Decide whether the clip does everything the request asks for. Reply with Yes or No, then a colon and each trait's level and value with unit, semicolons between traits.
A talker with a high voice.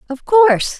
Yes: very high, 325 Hz